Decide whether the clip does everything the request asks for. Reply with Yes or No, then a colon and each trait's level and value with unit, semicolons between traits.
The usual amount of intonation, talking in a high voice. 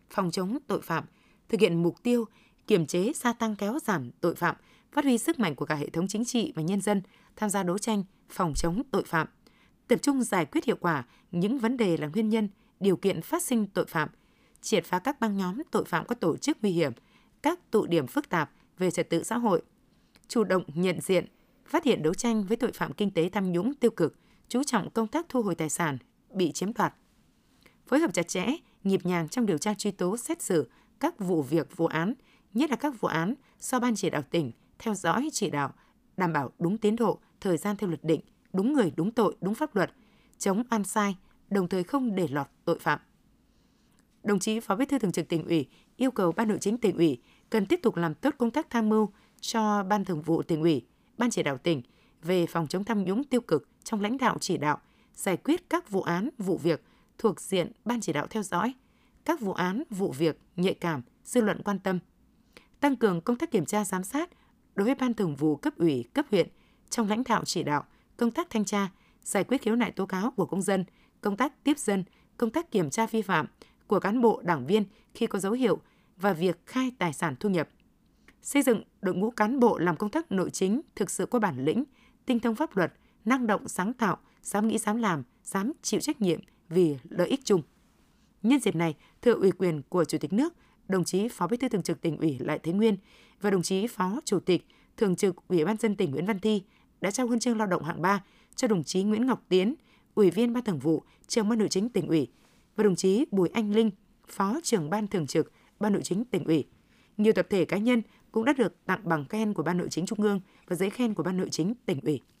Yes: average, 4.9 semitones; high, 205 Hz